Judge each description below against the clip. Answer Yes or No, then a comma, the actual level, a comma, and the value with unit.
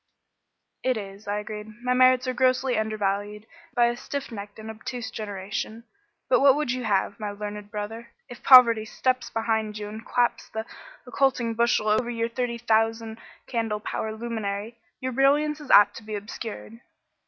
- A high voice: Yes, high, 225 Hz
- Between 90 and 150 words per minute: No, average, 165 wpm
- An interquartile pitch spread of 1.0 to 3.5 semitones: Yes, average, 2.8 semitones